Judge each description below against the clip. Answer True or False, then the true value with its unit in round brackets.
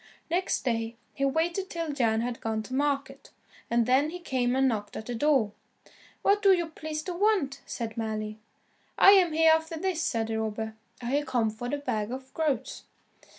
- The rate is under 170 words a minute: False (185 wpm)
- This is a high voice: True (270 Hz)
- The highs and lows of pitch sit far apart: True (6.0 semitones)